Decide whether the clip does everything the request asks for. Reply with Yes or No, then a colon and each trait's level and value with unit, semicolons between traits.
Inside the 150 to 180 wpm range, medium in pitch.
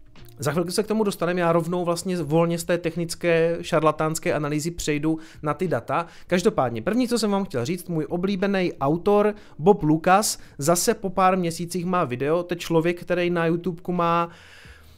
Yes: fast, 170 wpm; medium, 170 Hz